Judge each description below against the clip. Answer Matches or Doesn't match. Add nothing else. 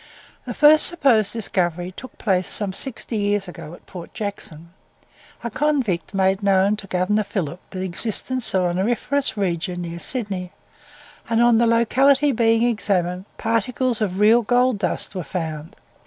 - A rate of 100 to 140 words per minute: Doesn't match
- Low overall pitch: Doesn't match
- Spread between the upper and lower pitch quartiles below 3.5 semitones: Doesn't match